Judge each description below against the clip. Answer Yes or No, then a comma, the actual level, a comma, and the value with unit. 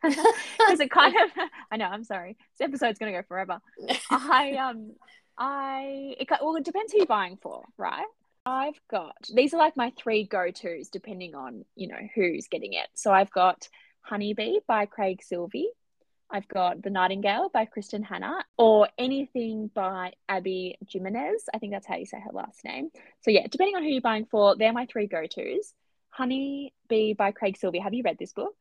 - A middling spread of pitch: No, wide, 5.7 semitones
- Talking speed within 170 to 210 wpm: Yes, average, 185 wpm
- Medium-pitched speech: No, high, 225 Hz